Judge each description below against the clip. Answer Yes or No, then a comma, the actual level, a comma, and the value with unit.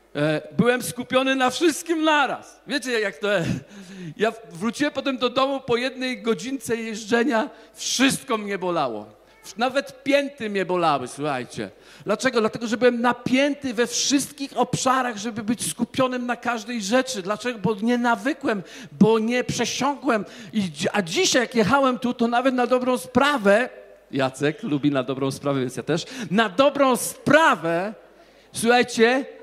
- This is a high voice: Yes, high, 235 Hz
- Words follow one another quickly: No, average, 140 wpm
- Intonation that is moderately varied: Yes, average, 4.5 semitones